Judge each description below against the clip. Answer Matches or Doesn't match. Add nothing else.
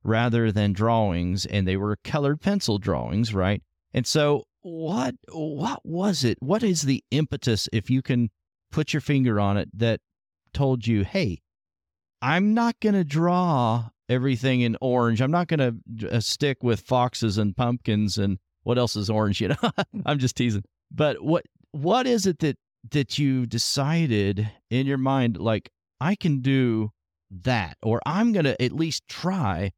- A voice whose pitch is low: Matches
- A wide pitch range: Matches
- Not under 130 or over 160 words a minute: Doesn't match